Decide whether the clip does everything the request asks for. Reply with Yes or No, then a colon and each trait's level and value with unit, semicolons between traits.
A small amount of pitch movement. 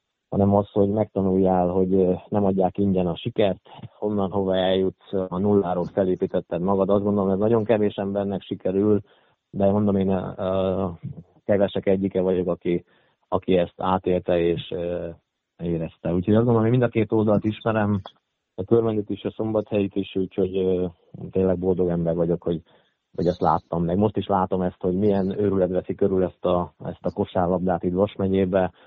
Yes: narrow, 1.9 semitones